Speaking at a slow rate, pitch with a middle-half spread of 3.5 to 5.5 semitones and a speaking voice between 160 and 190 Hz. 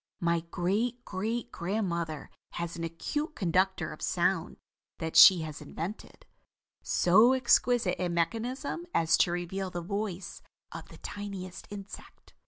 Yes: slow, 130 wpm; average, 4.2 semitones; medium, 185 Hz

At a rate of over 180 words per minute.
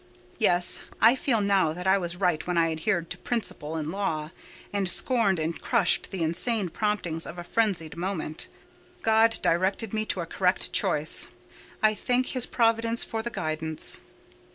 No: average, 165 wpm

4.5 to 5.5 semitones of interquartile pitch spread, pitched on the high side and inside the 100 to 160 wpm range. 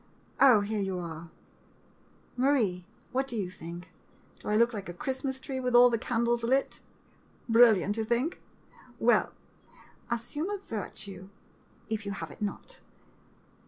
Yes: average, 4.8 semitones; high, 225 Hz; average, 155 wpm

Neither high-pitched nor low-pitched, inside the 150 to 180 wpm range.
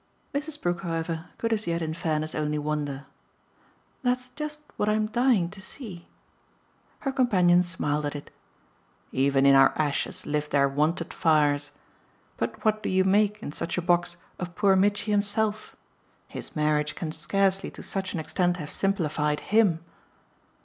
Yes: medium, 175 Hz; average, 155 wpm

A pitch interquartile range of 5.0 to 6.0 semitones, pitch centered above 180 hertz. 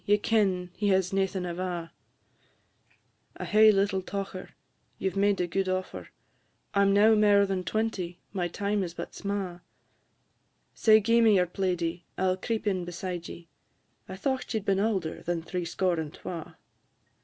No: narrow, 2.4 semitones; high, 190 Hz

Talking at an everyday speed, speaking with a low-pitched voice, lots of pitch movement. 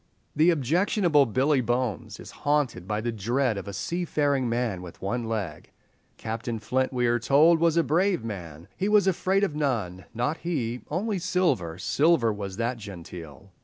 Yes: average, 165 wpm; low, 125 Hz; wide, 7.1 semitones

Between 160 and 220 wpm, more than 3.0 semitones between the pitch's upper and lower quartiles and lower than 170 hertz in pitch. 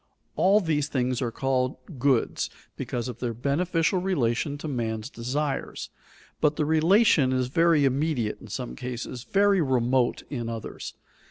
No: average, 145 wpm; average, 4.5 semitones; low, 135 Hz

